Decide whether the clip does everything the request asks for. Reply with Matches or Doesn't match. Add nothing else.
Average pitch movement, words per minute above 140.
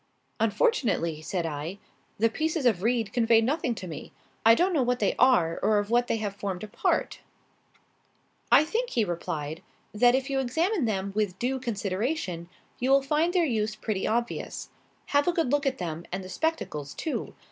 Doesn't match